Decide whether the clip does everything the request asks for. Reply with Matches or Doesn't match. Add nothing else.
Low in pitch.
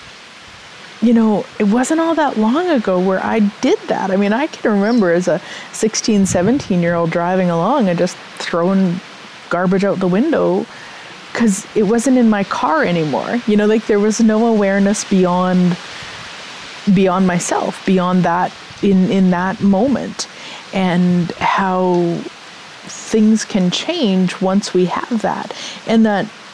Doesn't match